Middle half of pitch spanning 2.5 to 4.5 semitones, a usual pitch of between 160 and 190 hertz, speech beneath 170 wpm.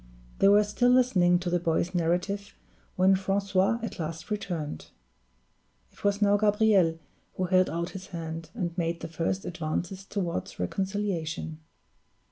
Yes: average, 3.1 semitones; medium, 185 Hz; average, 140 wpm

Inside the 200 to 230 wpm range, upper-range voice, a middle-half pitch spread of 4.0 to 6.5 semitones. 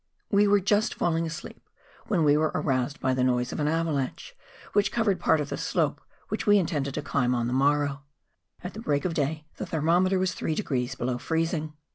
No: fast, 205 wpm; medium, 155 Hz; average, 4.7 semitones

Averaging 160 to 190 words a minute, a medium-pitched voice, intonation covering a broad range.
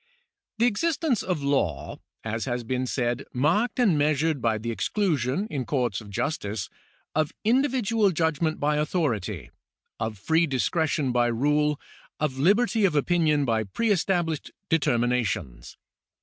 No: slow, 135 wpm; medium, 150 Hz; wide, 6.4 semitones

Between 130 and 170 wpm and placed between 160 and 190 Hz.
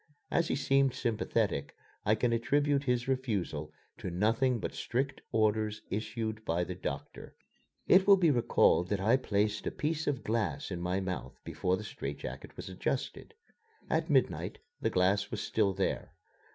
No: average, 165 wpm; low, 110 Hz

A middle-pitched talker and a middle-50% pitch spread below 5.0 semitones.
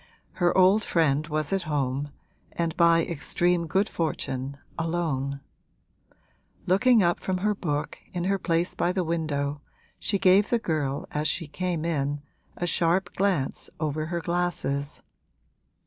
Yes: medium, 165 Hz; average, 3.7 semitones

